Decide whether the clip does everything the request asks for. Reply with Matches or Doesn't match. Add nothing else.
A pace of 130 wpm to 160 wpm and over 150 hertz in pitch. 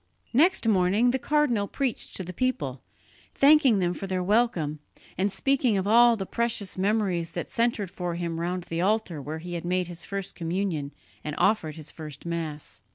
Doesn't match